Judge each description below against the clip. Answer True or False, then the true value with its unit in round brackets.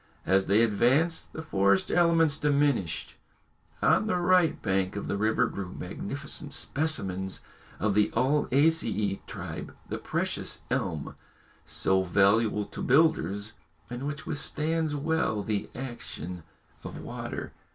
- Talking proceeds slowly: True (120 wpm)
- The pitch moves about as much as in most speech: False (7.7 semitones)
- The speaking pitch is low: True (120 Hz)